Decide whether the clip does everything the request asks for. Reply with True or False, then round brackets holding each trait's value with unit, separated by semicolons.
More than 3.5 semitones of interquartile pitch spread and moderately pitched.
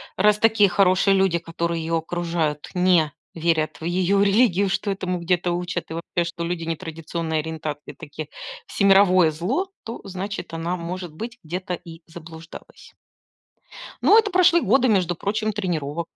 False (3.2 semitones; 175 Hz)